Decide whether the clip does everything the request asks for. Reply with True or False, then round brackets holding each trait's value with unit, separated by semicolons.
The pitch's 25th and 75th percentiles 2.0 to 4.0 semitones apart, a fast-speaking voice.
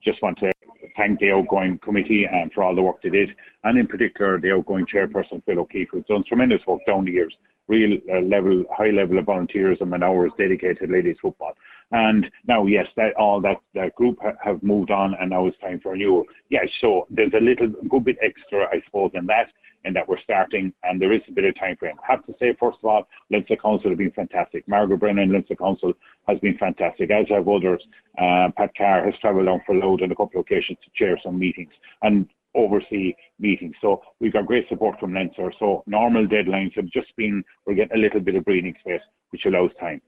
True (2.6 semitones; 230 wpm)